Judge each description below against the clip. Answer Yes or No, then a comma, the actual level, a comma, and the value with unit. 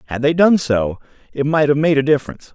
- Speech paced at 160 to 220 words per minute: No, fast, 235 wpm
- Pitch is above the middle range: No, medium, 145 Hz